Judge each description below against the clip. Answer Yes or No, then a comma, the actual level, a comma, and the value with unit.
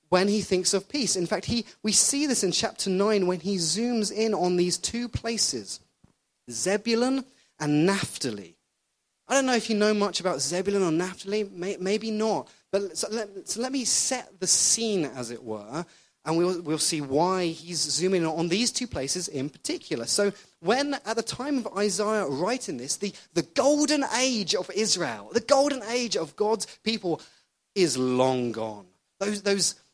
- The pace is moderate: Yes, average, 180 wpm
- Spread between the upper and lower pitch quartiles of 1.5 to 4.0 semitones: No, average, 4.7 semitones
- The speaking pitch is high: Yes, high, 195 Hz